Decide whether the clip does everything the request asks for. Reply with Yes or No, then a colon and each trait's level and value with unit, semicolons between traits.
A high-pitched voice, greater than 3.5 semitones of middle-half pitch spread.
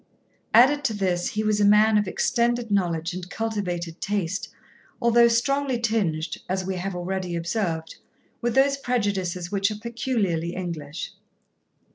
Yes: high, 200 Hz; average, 4.7 semitones